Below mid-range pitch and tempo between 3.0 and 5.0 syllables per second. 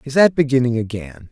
No: low, 130 Hz; 5.8 syllables/s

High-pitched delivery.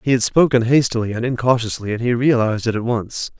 No: low, 120 Hz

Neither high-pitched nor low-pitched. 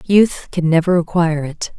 Yes: medium, 170 Hz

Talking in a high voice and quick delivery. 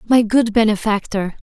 No: high, 220 Hz; slow, 120 wpm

